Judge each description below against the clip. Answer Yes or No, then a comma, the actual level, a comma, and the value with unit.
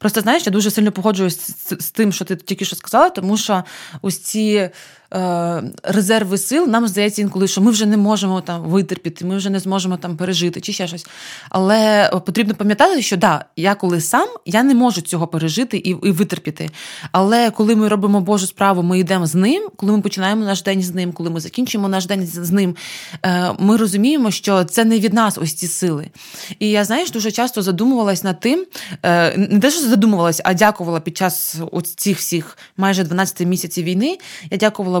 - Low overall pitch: No, high, 195 Hz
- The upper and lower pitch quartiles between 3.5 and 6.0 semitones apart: No, average, 3.1 semitones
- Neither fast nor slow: No, fast, 195 wpm